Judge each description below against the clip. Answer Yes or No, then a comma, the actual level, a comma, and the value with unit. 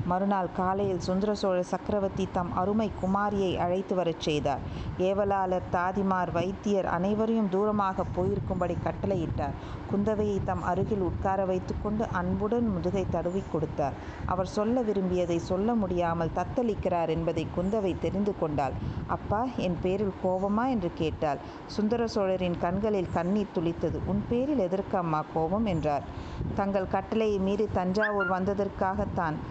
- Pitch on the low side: No, high, 190 Hz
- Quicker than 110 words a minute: Yes, average, 120 wpm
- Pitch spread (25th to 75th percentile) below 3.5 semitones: Yes, average, 2.9 semitones